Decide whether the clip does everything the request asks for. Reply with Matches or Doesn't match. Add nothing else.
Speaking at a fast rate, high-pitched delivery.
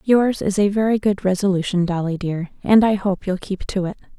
Matches